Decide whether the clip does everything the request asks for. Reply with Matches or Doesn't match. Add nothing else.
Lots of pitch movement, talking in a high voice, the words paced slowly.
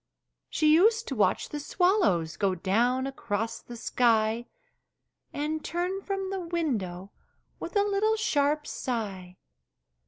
Matches